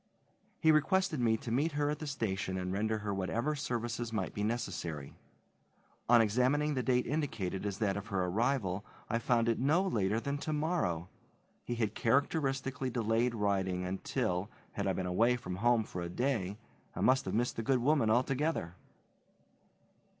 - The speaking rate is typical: Yes, average, 170 wpm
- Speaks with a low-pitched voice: Yes, low, 115 Hz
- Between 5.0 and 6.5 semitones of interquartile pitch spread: Yes, average, 5.3 semitones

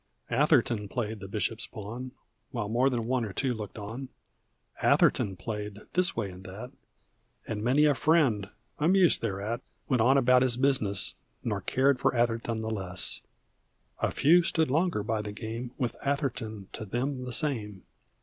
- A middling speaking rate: Yes, average, 160 wpm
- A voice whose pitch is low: Yes, low, 115 Hz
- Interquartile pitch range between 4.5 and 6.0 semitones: No, average, 4.1 semitones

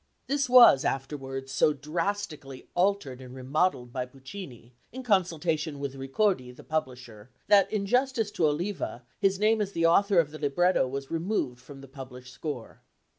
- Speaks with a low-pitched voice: No, medium, 150 Hz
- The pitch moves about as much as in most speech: No, wide, 6.7 semitones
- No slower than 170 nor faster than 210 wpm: No, average, 160 wpm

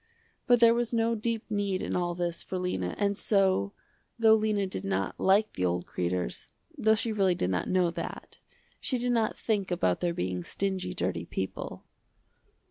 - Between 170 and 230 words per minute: Yes, average, 180 wpm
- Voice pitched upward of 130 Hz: Yes, high, 190 Hz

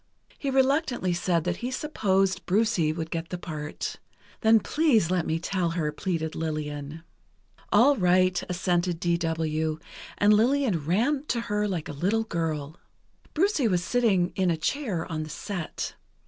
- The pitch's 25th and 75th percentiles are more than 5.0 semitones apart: Yes, wide, 5.5 semitones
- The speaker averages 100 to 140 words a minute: No, average, 155 wpm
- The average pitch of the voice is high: No, medium, 180 Hz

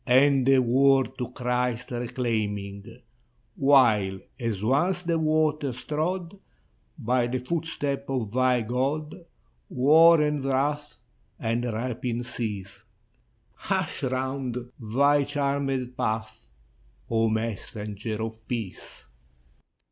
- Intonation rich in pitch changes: No, average, 3.7 semitones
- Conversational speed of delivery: No, slow, 100 wpm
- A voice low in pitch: Yes, low, 125 Hz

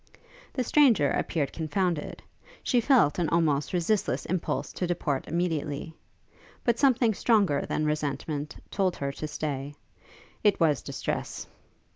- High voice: No, medium, 165 Hz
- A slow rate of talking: Yes, slow, 125 wpm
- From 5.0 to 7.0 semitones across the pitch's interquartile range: Yes, average, 5.3 semitones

